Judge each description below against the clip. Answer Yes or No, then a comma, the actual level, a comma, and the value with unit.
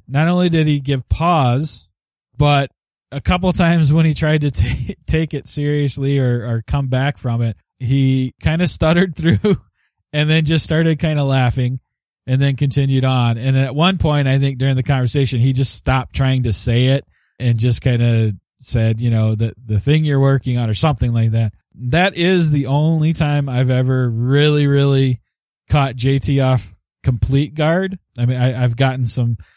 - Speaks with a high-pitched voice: No, low, 135 Hz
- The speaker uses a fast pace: No, average, 190 wpm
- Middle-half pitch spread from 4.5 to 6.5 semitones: No, average, 3.5 semitones